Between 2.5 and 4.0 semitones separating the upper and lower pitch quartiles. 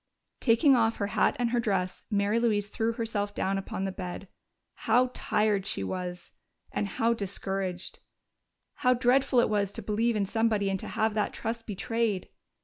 Yes: average, 2.9 semitones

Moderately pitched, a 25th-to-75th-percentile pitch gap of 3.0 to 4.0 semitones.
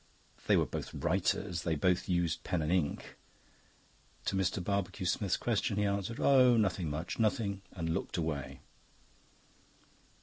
No: very low, 95 Hz; average, 3.5 semitones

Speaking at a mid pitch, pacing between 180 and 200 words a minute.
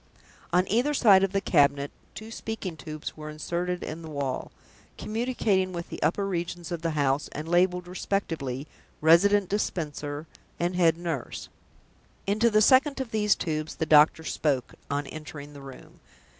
No: medium, 170 Hz; average, 155 wpm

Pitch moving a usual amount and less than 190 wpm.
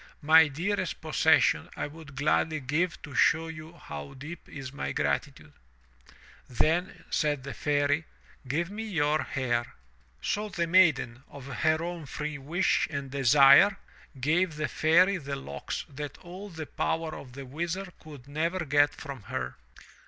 Yes: average, 3.3 semitones; average, 150 wpm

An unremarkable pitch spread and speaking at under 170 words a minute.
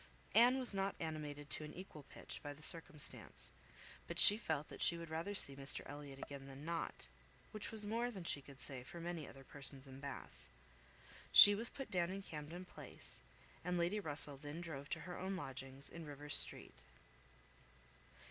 No: average, 4.6 semitones; average, 185 wpm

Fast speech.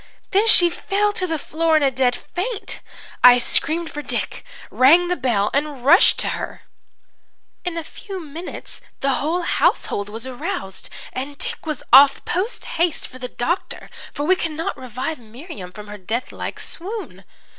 No: average, 165 wpm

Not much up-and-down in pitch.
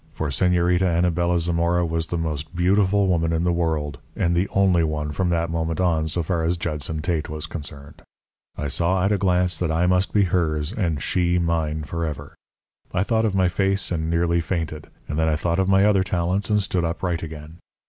Yes: narrow, 2.2 semitones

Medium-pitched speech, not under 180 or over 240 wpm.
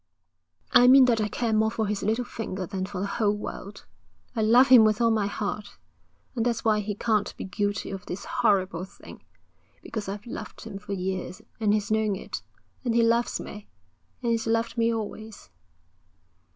No: high, 215 Hz; average, 190 wpm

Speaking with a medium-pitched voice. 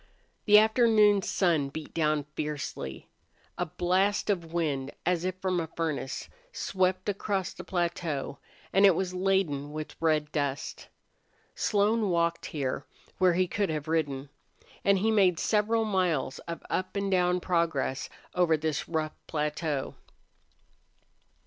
Yes: medium, 175 Hz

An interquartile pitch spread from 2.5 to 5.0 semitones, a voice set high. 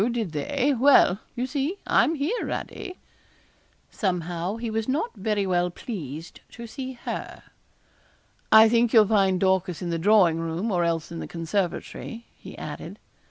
No: wide, 5.5 semitones; high, 205 Hz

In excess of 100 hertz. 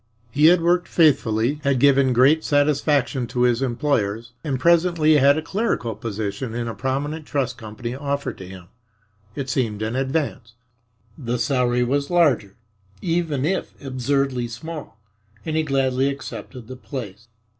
Yes: low, 135 Hz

